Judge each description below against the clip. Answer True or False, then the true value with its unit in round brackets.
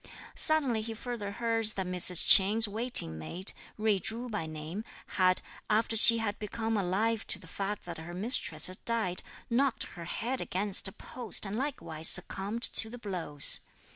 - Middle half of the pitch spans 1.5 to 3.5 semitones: False (3.9 semitones)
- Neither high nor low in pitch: False (210 Hz)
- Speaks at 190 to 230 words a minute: False (170 wpm)